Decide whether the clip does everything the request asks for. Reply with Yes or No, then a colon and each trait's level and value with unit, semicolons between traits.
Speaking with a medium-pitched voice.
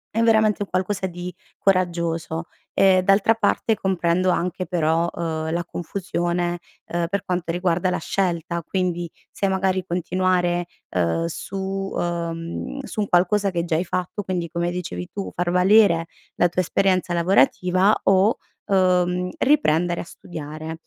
Yes: medium, 180 Hz